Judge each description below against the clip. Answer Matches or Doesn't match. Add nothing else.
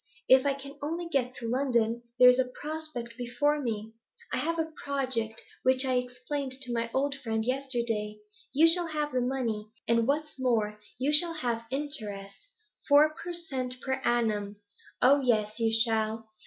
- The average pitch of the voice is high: Matches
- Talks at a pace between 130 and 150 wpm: Doesn't match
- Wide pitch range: Doesn't match